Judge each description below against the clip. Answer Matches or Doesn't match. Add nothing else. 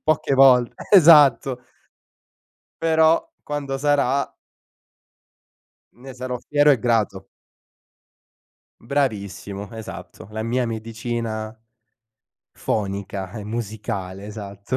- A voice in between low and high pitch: Doesn't match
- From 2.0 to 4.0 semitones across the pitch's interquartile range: Doesn't match